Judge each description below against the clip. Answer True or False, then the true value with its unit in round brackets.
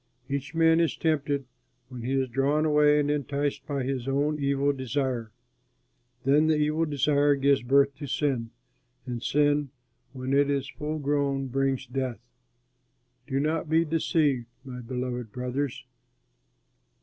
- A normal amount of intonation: False (2.1 semitones)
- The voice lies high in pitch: False (140 Hz)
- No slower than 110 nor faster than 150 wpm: True (140 wpm)